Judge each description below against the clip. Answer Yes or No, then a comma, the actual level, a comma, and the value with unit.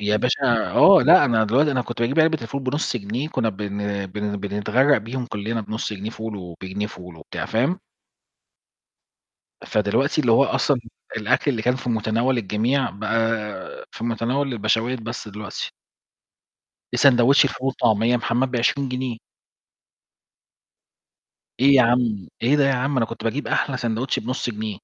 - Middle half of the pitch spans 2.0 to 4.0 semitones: Yes, average, 3.6 semitones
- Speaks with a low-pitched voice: Yes, low, 115 Hz